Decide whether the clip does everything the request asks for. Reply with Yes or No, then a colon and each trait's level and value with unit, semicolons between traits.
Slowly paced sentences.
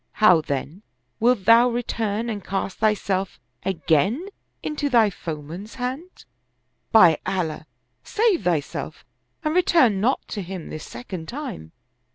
Yes: slow, 125 wpm